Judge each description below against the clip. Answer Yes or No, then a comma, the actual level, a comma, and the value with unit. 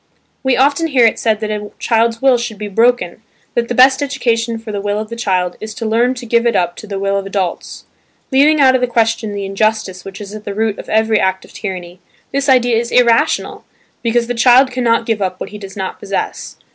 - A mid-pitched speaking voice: No, high, 225 Hz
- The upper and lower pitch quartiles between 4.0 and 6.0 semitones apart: No, average, 3.2 semitones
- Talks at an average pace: No, fast, 235 wpm